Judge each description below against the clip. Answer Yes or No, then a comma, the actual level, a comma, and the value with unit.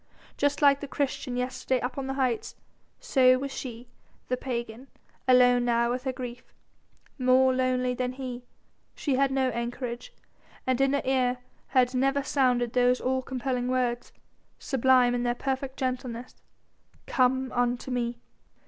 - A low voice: No, very high, 255 Hz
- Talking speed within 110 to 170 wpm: Yes, average, 150 wpm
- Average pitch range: No, narrow, 1.2 semitones